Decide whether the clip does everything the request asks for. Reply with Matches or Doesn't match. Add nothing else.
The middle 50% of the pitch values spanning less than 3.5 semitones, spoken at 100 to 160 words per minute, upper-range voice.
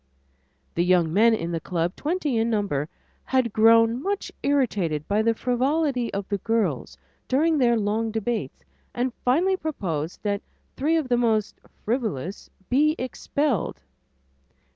Doesn't match